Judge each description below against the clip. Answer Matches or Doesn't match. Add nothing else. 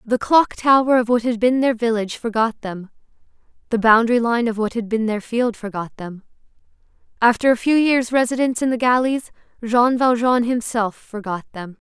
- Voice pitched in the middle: Doesn't match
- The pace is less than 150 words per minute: Doesn't match